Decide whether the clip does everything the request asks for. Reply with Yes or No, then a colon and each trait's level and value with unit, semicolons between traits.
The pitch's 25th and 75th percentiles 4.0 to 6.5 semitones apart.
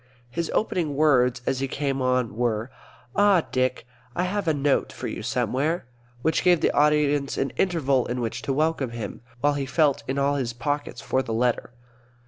No: average, 3.5 semitones